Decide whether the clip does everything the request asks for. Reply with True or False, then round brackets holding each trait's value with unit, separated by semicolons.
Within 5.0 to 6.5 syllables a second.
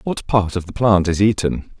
False (4.8 syllables/s)